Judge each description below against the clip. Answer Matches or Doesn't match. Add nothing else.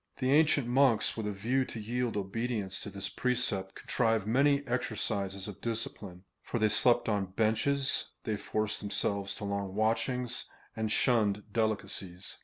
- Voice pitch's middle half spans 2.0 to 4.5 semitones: Matches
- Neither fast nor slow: Matches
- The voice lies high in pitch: Doesn't match